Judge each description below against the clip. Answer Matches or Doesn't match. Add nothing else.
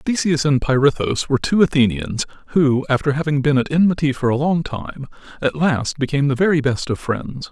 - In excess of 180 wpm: Matches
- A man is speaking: Matches